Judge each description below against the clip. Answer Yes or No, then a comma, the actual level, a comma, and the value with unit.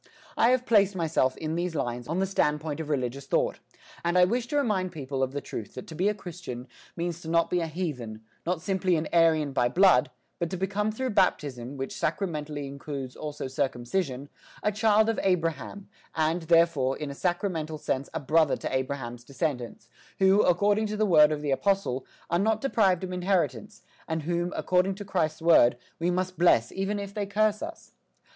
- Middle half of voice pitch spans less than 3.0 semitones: No, wide, 5.4 semitones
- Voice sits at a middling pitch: Yes, medium, 165 Hz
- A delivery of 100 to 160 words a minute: No, average, 195 wpm